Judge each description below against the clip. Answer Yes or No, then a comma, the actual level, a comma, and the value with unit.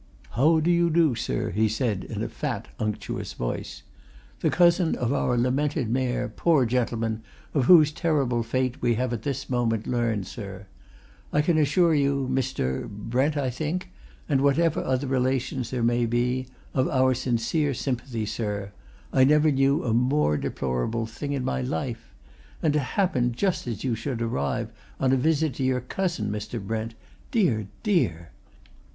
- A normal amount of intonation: Yes, average, 4.3 semitones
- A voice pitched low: Yes, low, 130 Hz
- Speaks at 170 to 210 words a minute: No, average, 160 wpm